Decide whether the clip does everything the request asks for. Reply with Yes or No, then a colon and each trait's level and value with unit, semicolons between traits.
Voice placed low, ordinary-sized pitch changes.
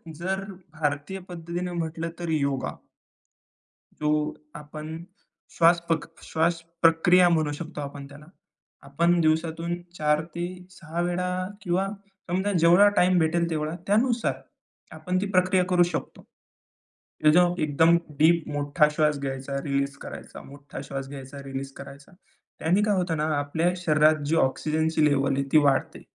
No: medium, 160 Hz; average, 3.1 semitones